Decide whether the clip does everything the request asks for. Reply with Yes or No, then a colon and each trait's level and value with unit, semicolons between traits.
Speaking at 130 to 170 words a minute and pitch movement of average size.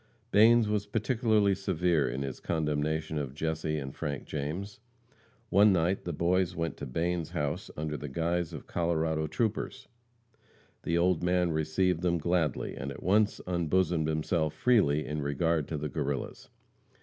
Yes: average, 150 wpm; average, 3.3 semitones